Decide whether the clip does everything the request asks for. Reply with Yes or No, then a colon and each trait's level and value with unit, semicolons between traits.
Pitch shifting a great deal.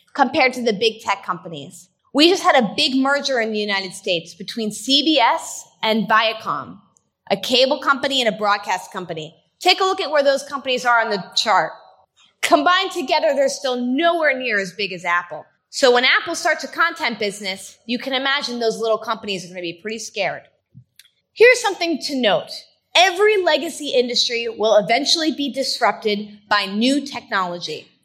Yes: wide, 5.7 semitones